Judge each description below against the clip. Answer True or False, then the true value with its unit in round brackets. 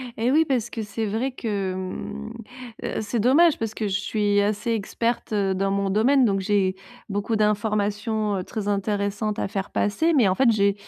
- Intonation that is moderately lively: False (2.2 semitones)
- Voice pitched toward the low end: False (210 Hz)